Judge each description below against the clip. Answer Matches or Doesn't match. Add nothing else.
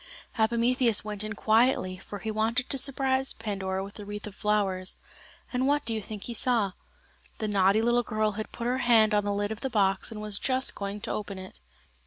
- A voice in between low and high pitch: Doesn't match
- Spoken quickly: Matches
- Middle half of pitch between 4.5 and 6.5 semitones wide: Doesn't match